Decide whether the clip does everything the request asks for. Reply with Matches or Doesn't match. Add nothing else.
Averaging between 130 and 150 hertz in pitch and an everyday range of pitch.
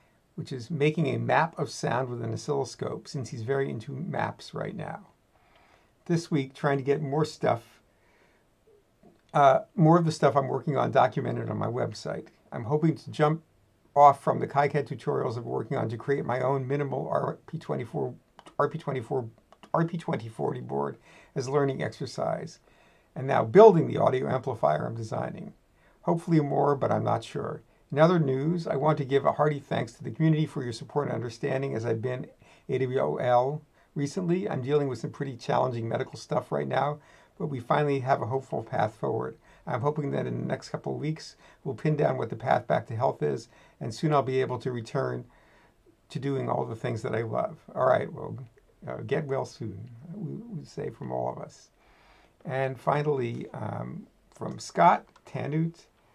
Matches